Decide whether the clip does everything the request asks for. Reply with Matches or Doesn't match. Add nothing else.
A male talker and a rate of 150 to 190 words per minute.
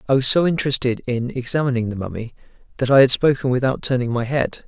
Doesn't match